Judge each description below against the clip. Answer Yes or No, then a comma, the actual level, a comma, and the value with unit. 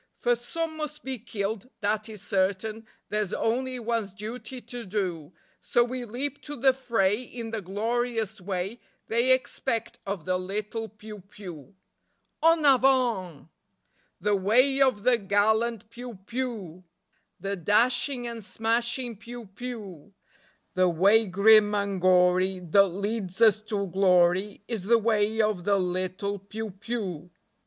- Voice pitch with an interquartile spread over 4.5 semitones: No, average, 3.7 semitones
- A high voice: Yes, high, 215 Hz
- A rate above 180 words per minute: No, average, 140 wpm